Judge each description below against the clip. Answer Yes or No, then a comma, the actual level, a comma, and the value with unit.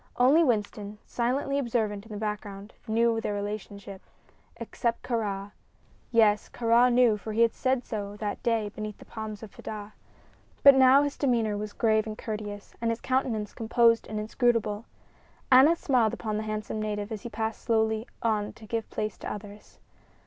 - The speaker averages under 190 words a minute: Yes, average, 170 wpm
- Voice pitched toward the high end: Yes, high, 220 Hz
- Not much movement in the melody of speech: Yes, narrow, 2.1 semitones